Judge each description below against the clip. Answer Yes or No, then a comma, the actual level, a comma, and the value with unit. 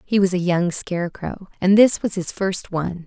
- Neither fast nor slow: No, fast, 215 wpm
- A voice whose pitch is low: No, medium, 185 Hz